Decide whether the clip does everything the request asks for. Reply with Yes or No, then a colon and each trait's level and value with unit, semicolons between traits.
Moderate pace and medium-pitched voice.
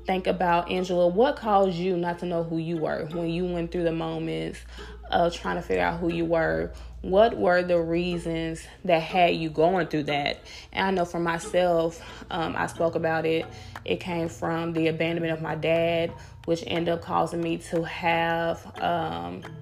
Yes: average, 190 wpm; medium, 165 Hz